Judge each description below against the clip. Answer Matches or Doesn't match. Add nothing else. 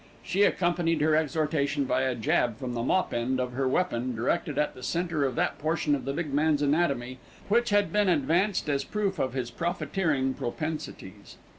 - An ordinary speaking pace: Matches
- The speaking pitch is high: Doesn't match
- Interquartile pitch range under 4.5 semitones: Doesn't match